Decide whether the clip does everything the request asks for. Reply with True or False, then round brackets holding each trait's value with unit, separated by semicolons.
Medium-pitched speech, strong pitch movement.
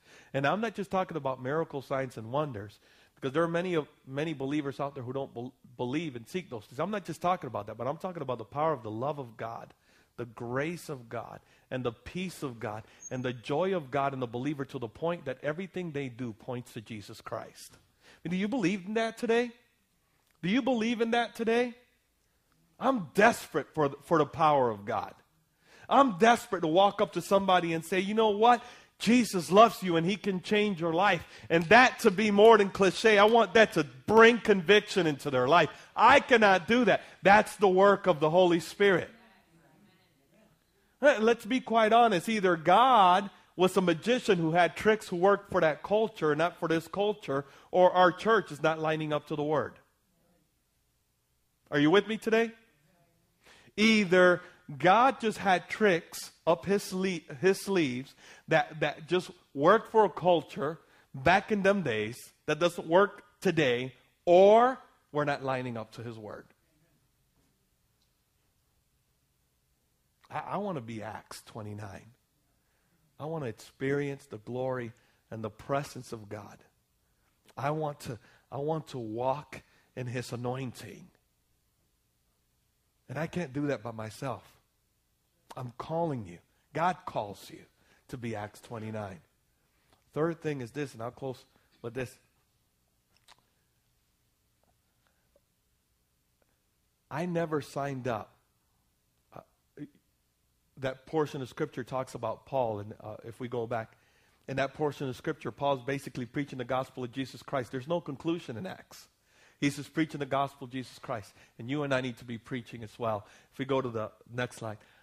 True (150 Hz; 7.1 semitones)